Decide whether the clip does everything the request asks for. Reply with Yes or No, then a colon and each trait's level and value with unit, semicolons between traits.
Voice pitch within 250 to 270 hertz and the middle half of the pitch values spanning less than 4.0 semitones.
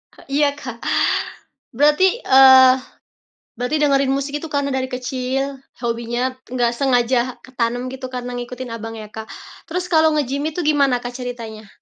Yes: very high, 255 Hz; narrow, 2.5 semitones